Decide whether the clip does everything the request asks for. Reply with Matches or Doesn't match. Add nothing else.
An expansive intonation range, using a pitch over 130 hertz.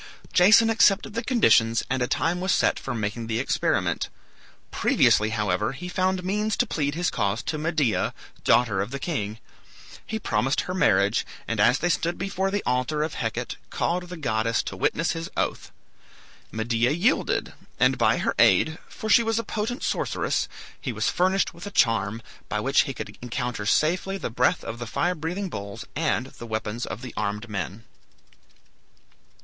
Matches